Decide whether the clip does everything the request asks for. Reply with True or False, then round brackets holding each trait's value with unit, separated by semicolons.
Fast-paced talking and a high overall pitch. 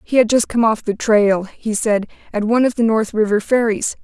True (240 wpm; 220 Hz)